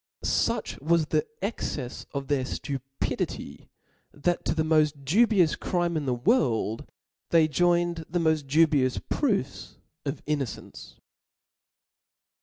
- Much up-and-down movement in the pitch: No, average, 3.9 semitones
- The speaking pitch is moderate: Yes, medium, 155 Hz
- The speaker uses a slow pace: Yes, slow, 120 wpm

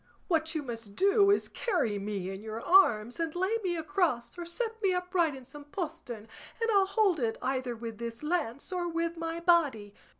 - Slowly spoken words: No, average, 195 wpm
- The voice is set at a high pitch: Yes, very high, 325 Hz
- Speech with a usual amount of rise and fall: No, wide, 7.5 semitones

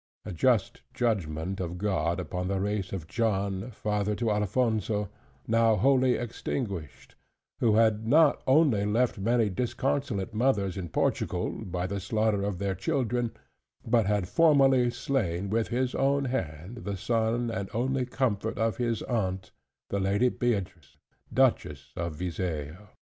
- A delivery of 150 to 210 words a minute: No, average, 140 wpm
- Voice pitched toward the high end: No, low, 105 Hz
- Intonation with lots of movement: No, average, 4.2 semitones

